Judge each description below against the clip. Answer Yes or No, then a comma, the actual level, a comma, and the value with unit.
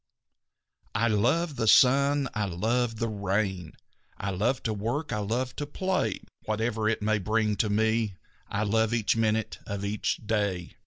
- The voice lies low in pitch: Yes, low, 110 Hz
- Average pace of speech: Yes, average, 160 wpm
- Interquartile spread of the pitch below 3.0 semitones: Yes, narrow, 2.6 semitones